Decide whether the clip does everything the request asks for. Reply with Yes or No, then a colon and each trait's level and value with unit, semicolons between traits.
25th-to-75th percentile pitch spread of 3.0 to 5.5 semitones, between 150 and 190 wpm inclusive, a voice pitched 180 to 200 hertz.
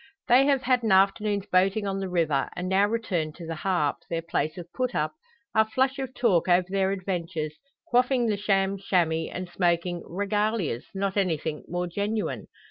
Yes: average, 3.8 semitones; average, 180 wpm; high, 190 Hz